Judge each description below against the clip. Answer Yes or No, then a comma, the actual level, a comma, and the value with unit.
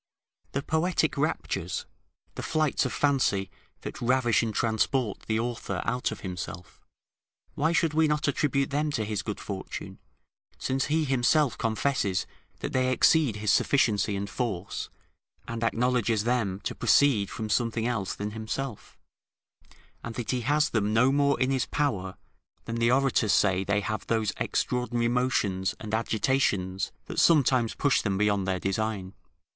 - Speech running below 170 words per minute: Yes, average, 150 wpm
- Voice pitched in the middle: No, low, 115 Hz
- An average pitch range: Yes, average, 4.6 semitones